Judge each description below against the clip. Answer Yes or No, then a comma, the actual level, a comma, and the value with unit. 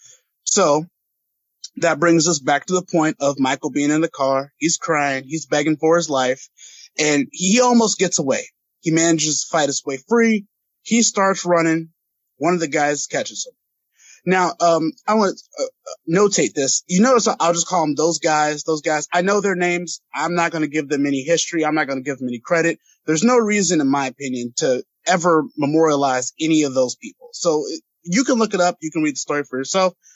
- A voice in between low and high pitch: Yes, medium, 165 Hz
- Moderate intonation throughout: Yes, average, 4.2 semitones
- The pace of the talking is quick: Yes, fast, 210 wpm